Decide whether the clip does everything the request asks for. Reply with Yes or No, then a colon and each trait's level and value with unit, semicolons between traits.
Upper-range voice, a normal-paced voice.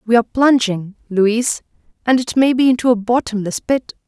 Yes: high, 235 Hz; average, 160 wpm